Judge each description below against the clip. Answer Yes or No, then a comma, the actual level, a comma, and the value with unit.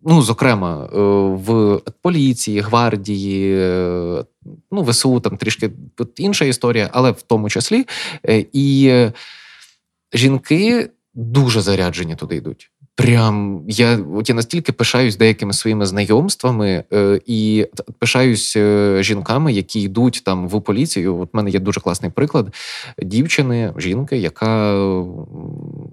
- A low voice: Yes, low, 110 Hz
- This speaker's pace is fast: No, average, 110 wpm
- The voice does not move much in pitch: No, average, 4.3 semitones